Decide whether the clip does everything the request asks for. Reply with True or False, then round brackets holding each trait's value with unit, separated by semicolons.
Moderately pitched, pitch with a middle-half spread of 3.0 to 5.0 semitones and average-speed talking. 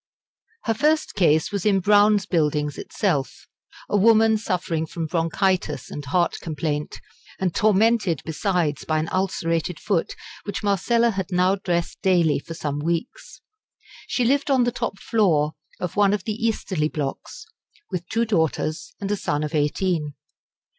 True (180 Hz; 4.7 semitones; 150 wpm)